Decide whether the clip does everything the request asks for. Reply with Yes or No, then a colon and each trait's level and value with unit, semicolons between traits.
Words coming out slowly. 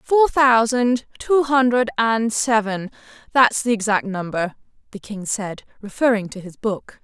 No: average, 145 wpm